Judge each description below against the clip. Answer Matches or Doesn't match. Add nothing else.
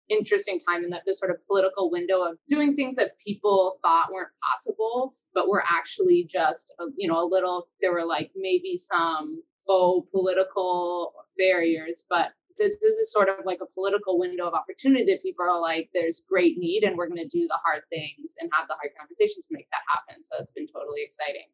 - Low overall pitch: Doesn't match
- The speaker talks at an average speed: Doesn't match